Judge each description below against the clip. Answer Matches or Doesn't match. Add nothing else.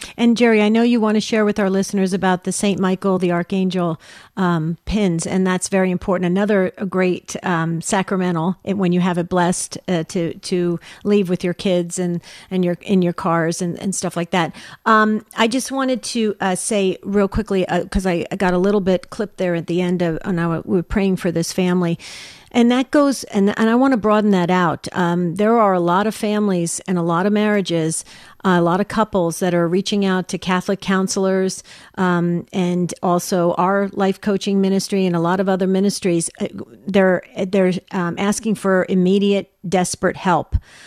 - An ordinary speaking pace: Matches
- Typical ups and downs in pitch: Doesn't match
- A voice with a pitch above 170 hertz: Matches